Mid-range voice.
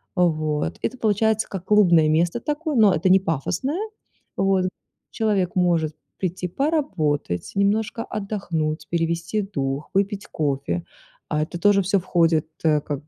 Yes: medium, 180 Hz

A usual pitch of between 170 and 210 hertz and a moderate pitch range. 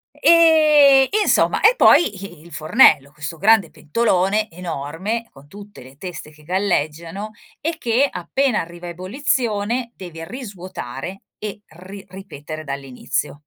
No: high, 190 Hz; wide, 6.6 semitones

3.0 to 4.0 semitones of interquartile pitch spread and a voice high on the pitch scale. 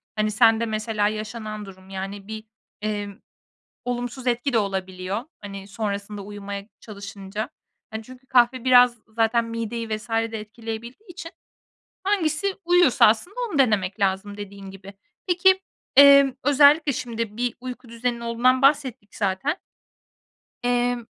Yes: average, 3.6 semitones; high, 225 Hz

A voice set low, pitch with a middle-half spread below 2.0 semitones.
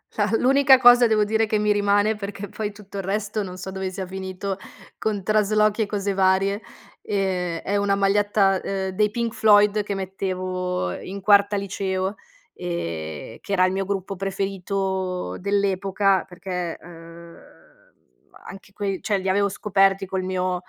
No: high, 195 Hz; narrow, 1.6 semitones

